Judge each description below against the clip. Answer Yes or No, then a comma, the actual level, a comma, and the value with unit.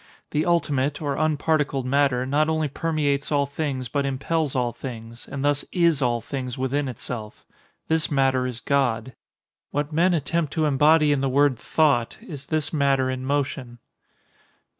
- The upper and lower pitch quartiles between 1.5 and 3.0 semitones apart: Yes, average, 2.7 semitones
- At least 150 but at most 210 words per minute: Yes, average, 160 wpm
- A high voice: No, medium, 140 Hz